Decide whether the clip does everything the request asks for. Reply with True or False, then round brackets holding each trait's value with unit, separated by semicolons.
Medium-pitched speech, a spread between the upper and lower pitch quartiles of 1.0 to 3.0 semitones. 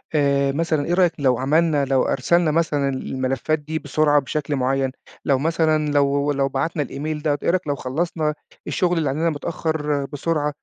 True (145 Hz; 2.5 semitones)